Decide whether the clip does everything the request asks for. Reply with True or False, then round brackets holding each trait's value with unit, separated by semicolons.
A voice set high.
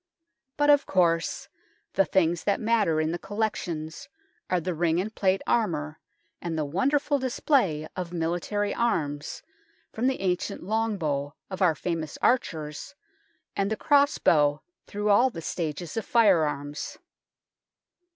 False (180 Hz)